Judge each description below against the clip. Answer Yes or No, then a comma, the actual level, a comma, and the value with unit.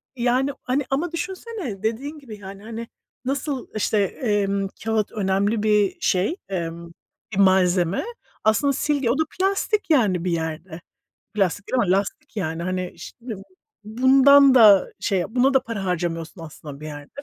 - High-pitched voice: Yes, high, 210 Hz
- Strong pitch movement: Yes, wide, 6.1 semitones